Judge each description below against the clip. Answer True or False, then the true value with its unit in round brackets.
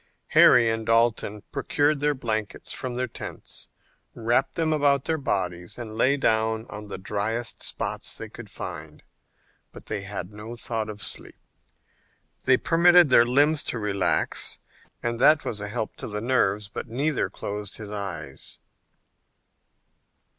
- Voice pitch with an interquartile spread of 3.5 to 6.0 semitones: True (4.2 semitones)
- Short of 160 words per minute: True (145 wpm)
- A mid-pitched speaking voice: False (115 Hz)